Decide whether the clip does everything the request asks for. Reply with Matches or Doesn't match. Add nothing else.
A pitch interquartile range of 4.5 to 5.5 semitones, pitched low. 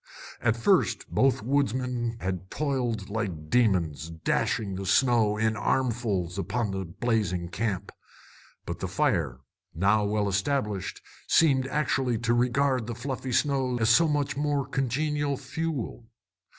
Matches